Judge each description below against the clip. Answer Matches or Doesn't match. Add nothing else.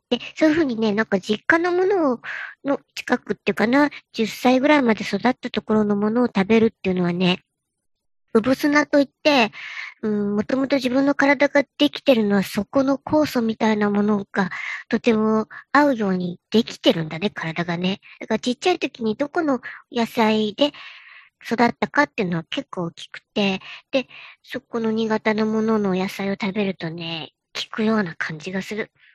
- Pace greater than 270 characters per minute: Matches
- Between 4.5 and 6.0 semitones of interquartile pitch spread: Matches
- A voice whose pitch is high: Matches